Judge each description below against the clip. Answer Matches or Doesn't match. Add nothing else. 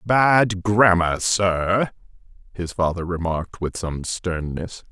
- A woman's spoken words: Doesn't match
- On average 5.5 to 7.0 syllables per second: Doesn't match